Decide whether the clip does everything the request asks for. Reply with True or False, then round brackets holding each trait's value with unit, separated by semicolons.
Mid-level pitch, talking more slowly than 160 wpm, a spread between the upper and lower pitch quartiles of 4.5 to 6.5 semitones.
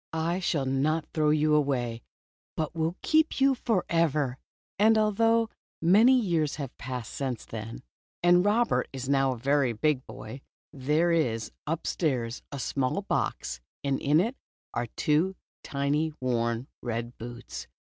True (150 Hz; 140 wpm; 5.3 semitones)